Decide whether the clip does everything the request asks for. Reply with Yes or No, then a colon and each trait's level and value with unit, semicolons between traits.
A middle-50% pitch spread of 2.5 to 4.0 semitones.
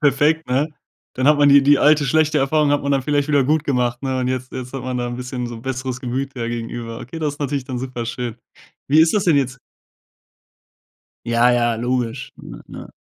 Yes: average, 2.9 semitones